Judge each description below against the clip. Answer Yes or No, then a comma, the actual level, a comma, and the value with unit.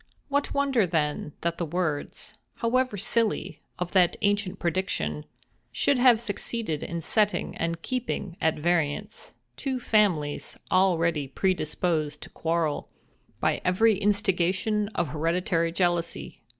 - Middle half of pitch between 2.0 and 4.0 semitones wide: No, average, 4.5 semitones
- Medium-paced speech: No, slow, 115 wpm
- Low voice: No, medium, 180 Hz